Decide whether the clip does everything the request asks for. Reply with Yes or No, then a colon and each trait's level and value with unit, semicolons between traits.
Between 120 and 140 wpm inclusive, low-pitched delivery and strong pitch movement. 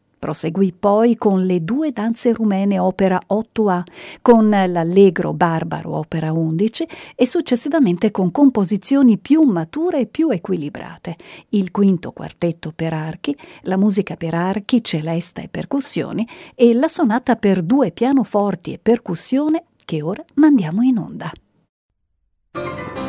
No: average, 125 wpm; high, 205 Hz; wide, 6.2 semitones